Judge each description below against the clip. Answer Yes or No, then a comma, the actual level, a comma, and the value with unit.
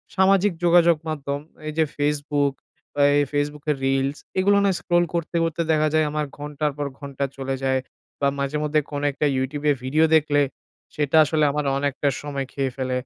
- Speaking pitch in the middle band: Yes, medium, 145 Hz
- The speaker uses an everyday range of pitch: No, narrow, 1.8 semitones